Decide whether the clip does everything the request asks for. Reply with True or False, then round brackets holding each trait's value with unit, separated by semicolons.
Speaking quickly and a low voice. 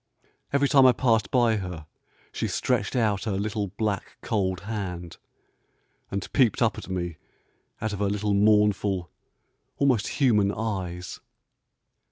False (135 wpm; 105 Hz)